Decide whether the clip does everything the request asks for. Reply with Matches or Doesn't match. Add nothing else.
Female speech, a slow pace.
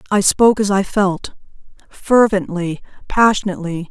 Matches